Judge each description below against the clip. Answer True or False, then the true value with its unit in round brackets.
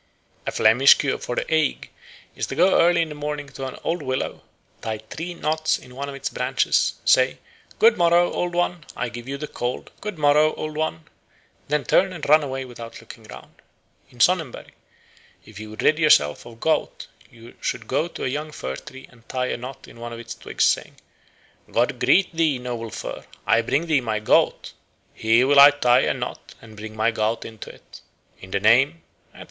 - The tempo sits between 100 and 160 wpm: False (205 wpm)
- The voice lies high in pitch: False (135 Hz)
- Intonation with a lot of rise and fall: False (4.9 semitones)